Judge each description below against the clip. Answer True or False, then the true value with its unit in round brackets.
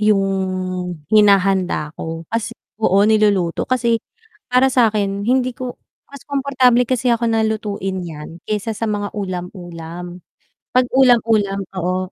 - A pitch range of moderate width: True (4.2 semitones)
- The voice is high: True (205 Hz)